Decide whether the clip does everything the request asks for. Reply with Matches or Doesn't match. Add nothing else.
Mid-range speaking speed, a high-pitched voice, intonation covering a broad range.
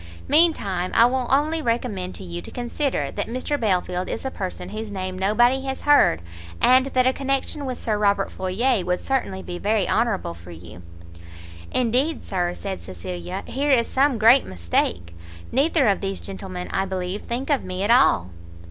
Matches